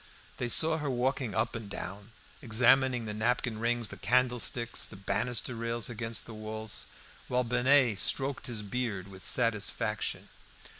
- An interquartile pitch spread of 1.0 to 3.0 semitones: Yes, narrow, 2.6 semitones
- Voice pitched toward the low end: Yes, low, 120 Hz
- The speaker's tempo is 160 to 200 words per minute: No, average, 145 wpm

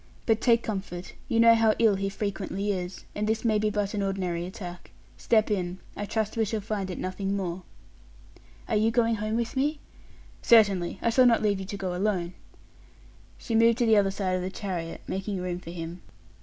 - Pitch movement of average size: Yes, average, 3.1 semitones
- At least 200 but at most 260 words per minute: Yes, fast, 205 wpm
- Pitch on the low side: No, high, 200 Hz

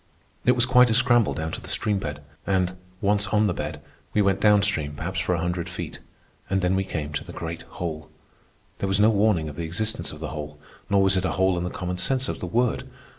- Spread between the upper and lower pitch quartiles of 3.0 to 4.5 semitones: Yes, average, 4.1 semitones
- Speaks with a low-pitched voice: Yes, very low, 95 Hz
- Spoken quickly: Yes, fast, 245 wpm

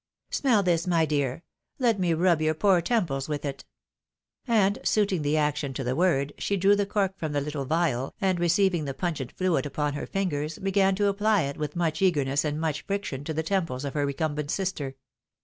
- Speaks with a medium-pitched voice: Yes, medium, 160 Hz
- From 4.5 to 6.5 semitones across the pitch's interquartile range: Yes, average, 4.9 semitones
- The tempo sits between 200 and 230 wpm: Yes, fast, 205 wpm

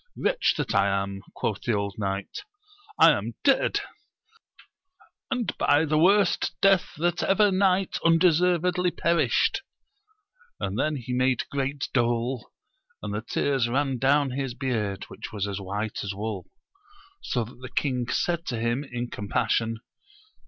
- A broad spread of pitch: Yes, wide, 7.0 semitones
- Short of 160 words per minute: Yes, average, 145 wpm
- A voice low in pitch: Yes, low, 130 Hz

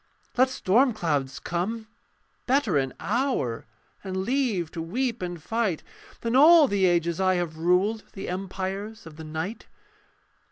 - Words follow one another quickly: No, average, 145 wpm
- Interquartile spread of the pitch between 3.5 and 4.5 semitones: No, average, 5.3 semitones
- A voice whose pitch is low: No, high, 190 Hz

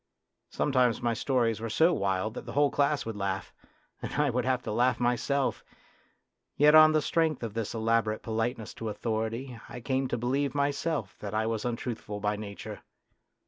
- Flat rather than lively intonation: No, average, 4.0 semitones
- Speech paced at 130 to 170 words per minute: No, average, 180 wpm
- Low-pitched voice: Yes, low, 120 Hz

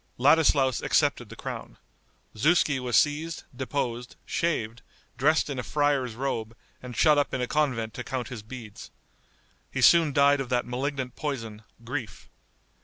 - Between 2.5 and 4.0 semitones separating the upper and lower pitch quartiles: Yes, average, 3.1 semitones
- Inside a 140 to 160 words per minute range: Yes, average, 150 wpm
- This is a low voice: Yes, low, 130 Hz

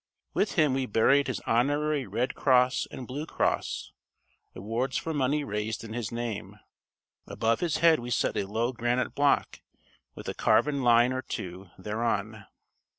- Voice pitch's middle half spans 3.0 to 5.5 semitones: Yes, average, 3.8 semitones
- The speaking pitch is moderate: No, low, 120 Hz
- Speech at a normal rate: Yes, average, 155 wpm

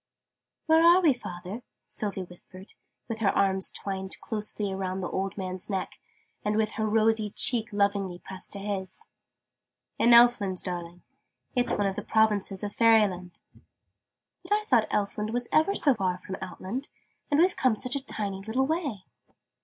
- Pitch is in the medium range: No, high, 210 Hz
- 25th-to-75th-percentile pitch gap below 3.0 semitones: No, average, 3.8 semitones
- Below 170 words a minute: Yes, average, 160 wpm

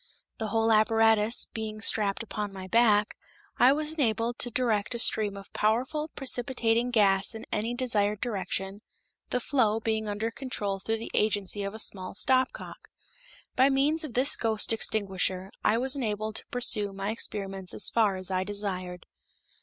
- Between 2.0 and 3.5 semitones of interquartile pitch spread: Yes, average, 3.0 semitones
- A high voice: Yes, high, 220 Hz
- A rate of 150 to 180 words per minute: Yes, average, 160 wpm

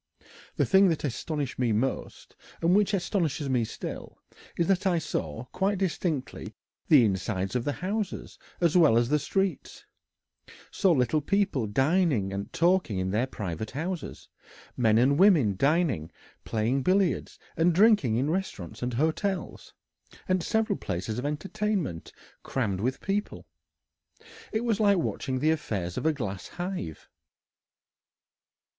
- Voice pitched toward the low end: No, medium, 150 Hz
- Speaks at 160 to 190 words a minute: No, average, 140 wpm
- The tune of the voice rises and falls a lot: Yes, wide, 8.3 semitones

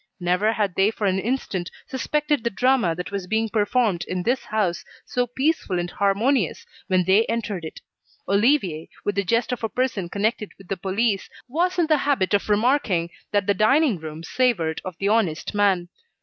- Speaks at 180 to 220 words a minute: Yes, average, 185 wpm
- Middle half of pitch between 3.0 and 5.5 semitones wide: Yes, average, 5.0 semitones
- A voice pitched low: No, high, 205 Hz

